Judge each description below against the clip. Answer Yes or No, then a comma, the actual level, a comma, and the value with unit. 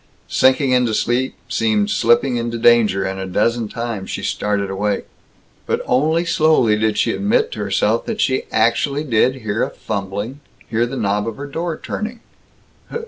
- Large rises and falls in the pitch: No, average, 4.4 semitones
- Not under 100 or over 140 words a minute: No, average, 165 wpm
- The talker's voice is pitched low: Yes, low, 120 Hz